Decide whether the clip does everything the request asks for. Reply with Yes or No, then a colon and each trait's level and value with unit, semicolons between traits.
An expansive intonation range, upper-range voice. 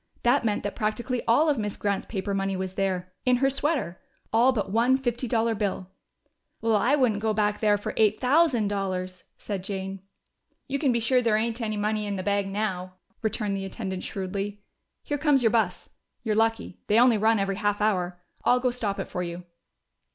No: average, 3.3 semitones; high, 215 Hz